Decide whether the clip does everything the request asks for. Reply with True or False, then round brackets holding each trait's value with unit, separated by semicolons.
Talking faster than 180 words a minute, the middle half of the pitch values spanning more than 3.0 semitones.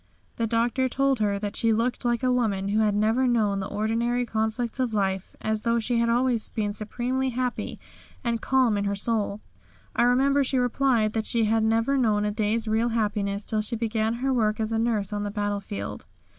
False (205 wpm; 2.4 semitones)